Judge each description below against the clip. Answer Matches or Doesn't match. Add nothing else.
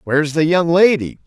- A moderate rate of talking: Matches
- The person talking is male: Matches